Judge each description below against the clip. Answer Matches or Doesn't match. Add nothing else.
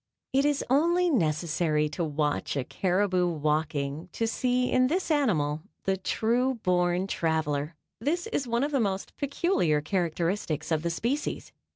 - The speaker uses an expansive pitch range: Matches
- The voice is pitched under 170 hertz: Doesn't match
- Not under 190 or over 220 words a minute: Doesn't match